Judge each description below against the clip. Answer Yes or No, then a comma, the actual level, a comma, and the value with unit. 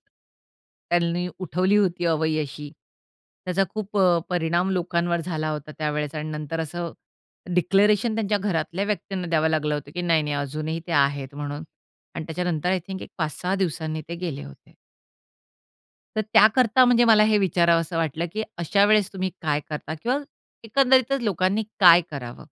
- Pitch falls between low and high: Yes, medium, 170 Hz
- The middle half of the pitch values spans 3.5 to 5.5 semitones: Yes, average, 4.0 semitones